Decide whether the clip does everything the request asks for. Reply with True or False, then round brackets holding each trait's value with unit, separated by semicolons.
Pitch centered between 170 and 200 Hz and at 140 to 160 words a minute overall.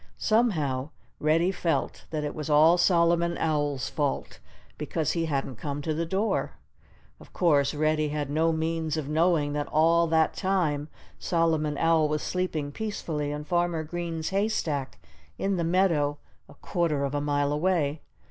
False (160 Hz; 155 wpm)